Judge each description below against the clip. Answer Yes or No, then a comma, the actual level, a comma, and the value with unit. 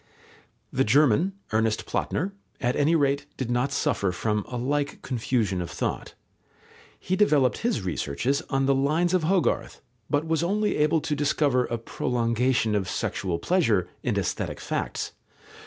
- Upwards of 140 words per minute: Yes, average, 150 wpm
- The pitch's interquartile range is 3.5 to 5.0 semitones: No, wide, 5.4 semitones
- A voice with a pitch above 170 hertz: No, low, 135 Hz